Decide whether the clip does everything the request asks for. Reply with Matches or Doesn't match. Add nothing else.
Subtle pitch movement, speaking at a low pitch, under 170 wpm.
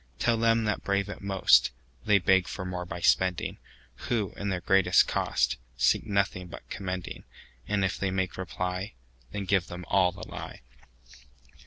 Matches